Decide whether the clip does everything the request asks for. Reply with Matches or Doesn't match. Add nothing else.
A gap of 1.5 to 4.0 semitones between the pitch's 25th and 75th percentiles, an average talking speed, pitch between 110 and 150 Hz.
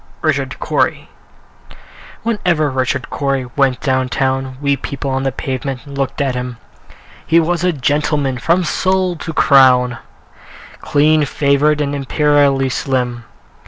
Doesn't match